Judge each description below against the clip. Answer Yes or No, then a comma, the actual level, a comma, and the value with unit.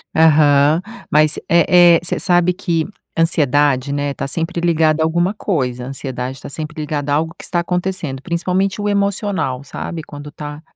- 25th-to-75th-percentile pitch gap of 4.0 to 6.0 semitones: No, average, 3.3 semitones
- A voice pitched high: No, medium, 160 Hz